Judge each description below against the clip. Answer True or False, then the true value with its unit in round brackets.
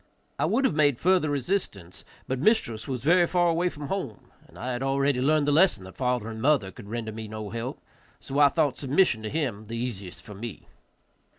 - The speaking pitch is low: True (130 Hz)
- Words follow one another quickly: True (210 wpm)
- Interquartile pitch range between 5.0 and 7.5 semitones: True (5.6 semitones)